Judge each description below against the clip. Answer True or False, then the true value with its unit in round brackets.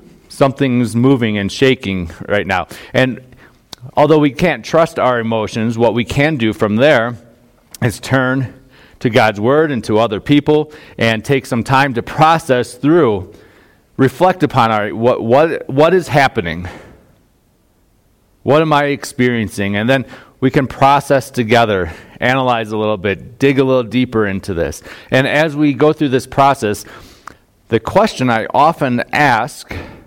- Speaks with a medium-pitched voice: False (125 Hz)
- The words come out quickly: False (150 wpm)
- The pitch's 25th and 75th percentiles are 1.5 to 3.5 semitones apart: False (3.9 semitones)